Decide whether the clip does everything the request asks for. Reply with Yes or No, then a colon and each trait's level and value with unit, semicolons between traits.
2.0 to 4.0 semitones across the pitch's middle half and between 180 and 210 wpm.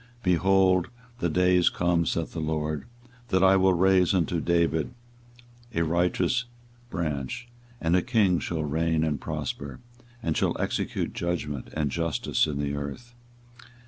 No: average, 2.9 semitones; average, 145 wpm